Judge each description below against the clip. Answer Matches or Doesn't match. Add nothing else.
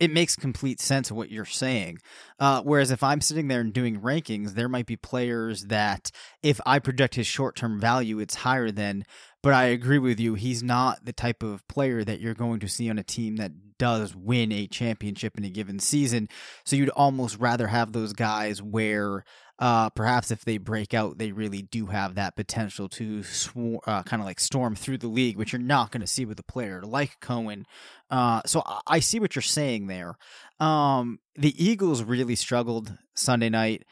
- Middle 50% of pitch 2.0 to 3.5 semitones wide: Matches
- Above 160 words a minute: Matches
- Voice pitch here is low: Matches